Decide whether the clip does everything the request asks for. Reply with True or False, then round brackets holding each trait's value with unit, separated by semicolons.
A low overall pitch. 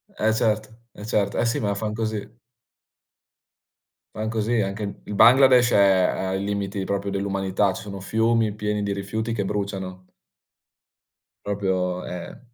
True (105 Hz)